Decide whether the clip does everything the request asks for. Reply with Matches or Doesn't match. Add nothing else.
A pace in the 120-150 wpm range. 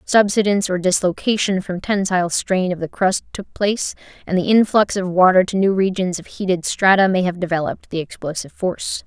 Doesn't match